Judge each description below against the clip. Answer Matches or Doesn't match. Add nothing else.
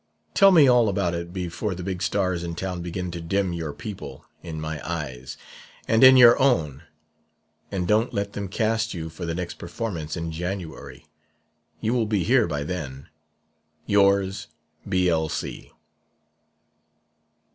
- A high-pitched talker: Doesn't match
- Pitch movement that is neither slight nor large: Matches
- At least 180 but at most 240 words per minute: Doesn't match